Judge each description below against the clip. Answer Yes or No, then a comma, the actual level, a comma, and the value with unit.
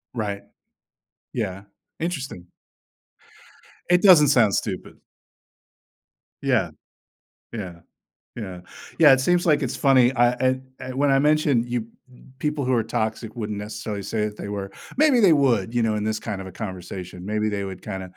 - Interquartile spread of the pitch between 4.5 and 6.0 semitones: Yes, average, 5.0 semitones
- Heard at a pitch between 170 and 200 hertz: No, low, 115 Hz